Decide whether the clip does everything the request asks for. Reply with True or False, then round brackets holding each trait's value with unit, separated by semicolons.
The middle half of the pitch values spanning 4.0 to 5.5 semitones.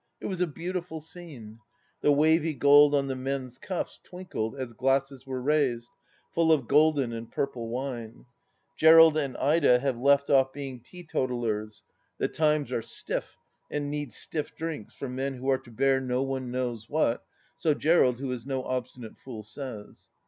False (3.3 semitones)